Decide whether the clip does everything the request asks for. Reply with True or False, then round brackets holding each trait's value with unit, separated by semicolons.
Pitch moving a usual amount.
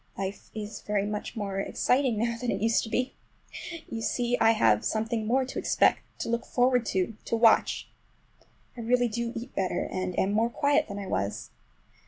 True (3.1 semitones)